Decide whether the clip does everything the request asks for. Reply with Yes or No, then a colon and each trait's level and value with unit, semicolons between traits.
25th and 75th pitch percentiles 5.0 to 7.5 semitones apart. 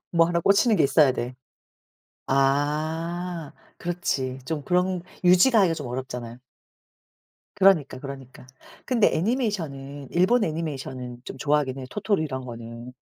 Yes: average, 5.3 semitones